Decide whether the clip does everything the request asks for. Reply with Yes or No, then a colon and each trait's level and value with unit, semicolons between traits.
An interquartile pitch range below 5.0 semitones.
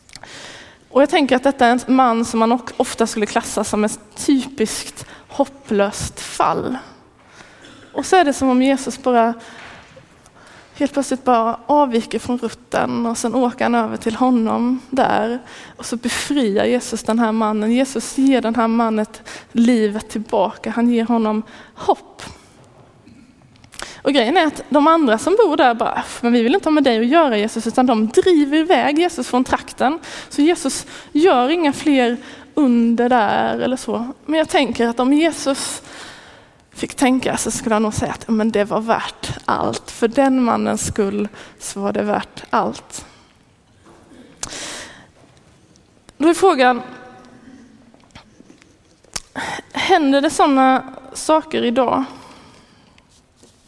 Yes: average, 3.5 semitones